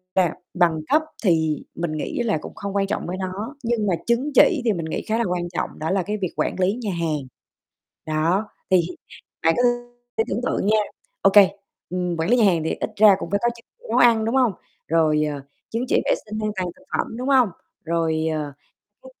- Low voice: No, high, 195 Hz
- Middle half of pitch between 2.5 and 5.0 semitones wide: No, wide, 5.6 semitones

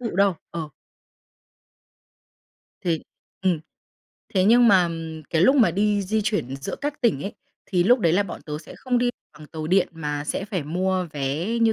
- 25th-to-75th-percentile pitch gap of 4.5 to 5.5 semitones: Yes, average, 5.2 semitones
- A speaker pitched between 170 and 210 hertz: Yes, medium, 185 Hz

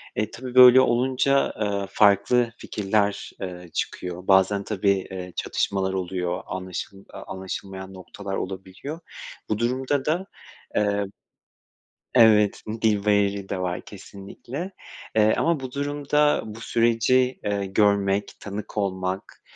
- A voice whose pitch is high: No, low, 100 Hz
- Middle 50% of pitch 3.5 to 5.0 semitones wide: Yes, average, 4.2 semitones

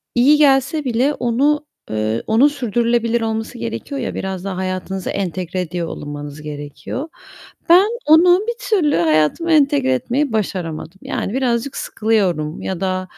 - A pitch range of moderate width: No, wide, 8.1 semitones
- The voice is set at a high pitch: Yes, high, 220 Hz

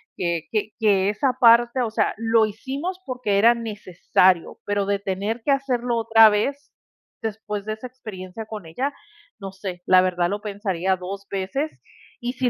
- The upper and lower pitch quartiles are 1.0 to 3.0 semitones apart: No, average, 3.6 semitones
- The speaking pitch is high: Yes, high, 215 Hz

